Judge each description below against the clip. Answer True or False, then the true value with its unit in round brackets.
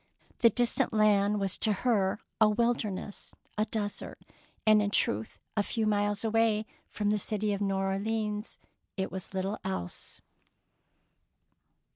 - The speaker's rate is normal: True (145 wpm)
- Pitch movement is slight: True (1.7 semitones)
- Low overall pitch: False (210 Hz)